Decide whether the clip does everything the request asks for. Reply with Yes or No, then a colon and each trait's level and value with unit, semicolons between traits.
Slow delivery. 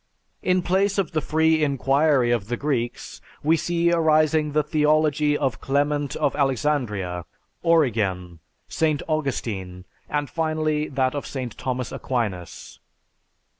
Yes: slow, 125 wpm